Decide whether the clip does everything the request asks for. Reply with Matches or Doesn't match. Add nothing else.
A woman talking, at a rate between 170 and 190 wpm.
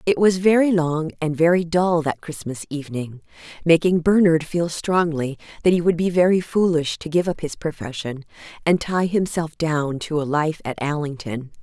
Matches